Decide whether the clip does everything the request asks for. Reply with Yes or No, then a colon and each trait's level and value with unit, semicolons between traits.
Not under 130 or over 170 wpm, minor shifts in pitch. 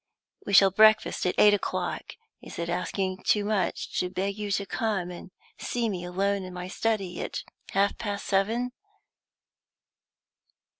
Yes: average, 150 wpm; narrow, 2.3 semitones